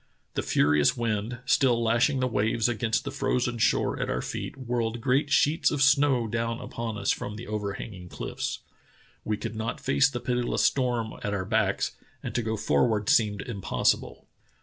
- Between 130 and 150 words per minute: No, average, 175 wpm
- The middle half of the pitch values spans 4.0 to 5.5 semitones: No, average, 2.8 semitones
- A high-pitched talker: No, low, 115 Hz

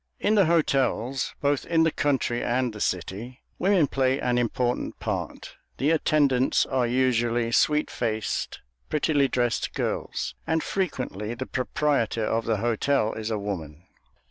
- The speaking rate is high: No, average, 145 wpm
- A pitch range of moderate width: Yes, average, 4.0 semitones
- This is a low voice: Yes, low, 125 Hz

